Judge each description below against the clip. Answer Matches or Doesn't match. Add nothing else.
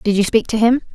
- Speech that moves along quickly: Matches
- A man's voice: Doesn't match